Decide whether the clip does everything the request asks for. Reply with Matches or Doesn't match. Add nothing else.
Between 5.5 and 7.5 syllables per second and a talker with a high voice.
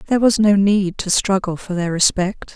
Doesn't match